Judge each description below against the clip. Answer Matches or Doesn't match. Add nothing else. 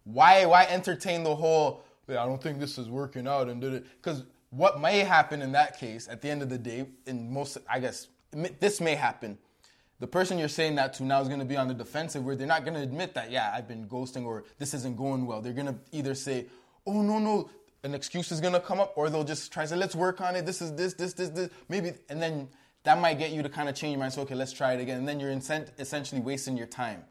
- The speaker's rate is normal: Doesn't match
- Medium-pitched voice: Matches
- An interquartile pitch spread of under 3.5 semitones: Doesn't match